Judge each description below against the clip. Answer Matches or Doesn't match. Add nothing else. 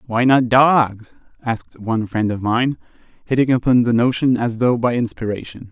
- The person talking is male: Matches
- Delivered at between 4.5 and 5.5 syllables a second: Matches